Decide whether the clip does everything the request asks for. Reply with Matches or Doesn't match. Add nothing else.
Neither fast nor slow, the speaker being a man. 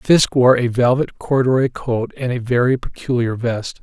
Matches